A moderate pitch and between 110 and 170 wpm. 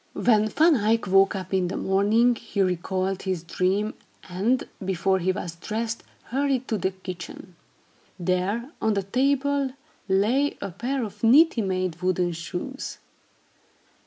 No: high, 200 Hz; average, 140 wpm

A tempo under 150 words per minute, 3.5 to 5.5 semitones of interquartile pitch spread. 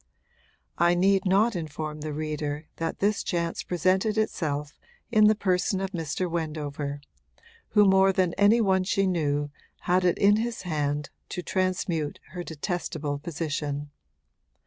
Yes: average, 140 wpm; average, 4.1 semitones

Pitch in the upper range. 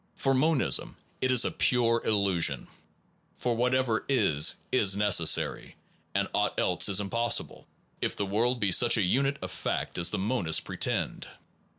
No: low, 110 Hz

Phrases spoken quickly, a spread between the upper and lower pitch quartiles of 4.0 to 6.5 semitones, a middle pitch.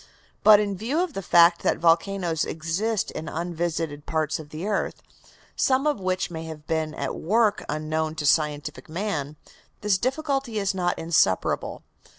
No: average, 160 wpm; average, 4.8 semitones; medium, 170 Hz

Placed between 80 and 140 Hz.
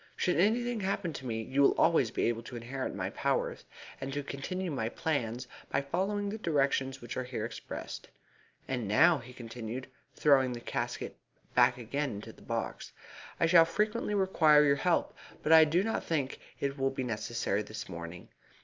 Yes: low, 135 Hz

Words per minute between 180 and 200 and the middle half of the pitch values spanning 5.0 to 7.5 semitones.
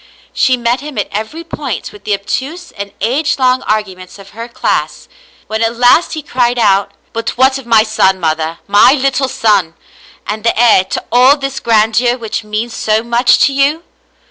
No: average, 190 wpm; average, 3.8 semitones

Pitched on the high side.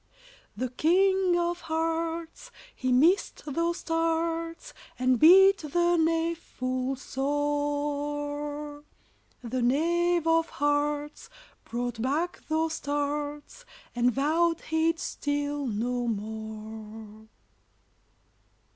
Yes: very high, 295 Hz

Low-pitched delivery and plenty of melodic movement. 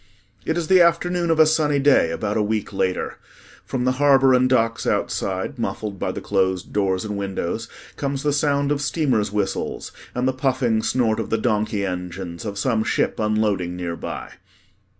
Yes: low, 110 Hz; wide, 5.9 semitones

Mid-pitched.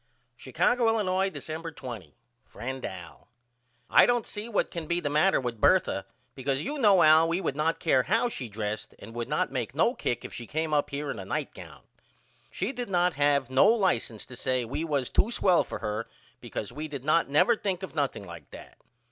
Yes: medium, 150 Hz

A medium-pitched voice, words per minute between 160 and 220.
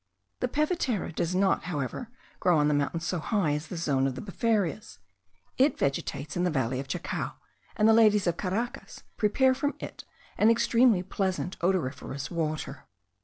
Yes: medium, 180 Hz; average, 170 wpm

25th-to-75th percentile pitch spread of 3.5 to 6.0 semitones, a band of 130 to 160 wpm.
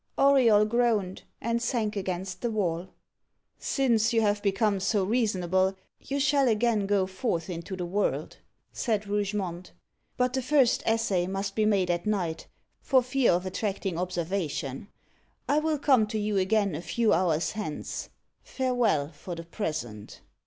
Yes: average, 4.2 semitones; average, 150 wpm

